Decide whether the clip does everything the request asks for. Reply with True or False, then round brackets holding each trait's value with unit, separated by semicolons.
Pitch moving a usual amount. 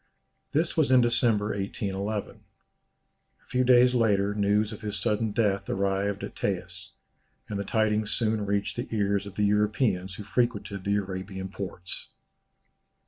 False (2.0 semitones)